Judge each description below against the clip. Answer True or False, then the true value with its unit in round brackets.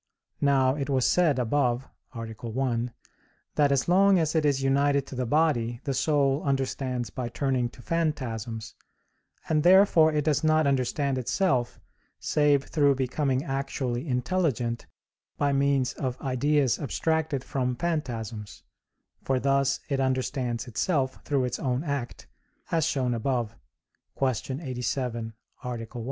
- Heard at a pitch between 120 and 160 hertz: True (135 Hz)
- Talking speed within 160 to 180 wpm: False (135 wpm)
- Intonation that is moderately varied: True (3.0 semitones)